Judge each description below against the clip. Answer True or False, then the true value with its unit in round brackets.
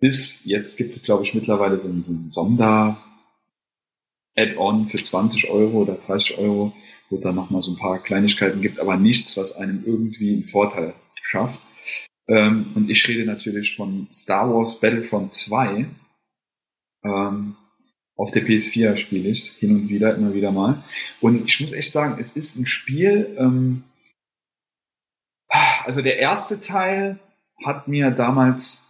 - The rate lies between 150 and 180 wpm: True (155 wpm)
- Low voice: True (110 Hz)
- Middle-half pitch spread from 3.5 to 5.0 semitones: True (4.0 semitones)